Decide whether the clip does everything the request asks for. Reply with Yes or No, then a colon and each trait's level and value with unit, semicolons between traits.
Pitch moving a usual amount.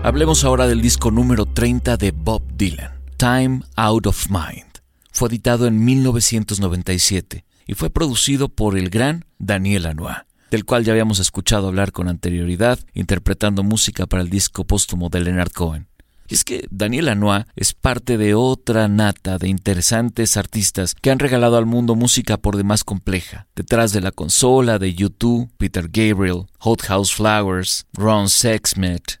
Yes: average, 3.9 semitones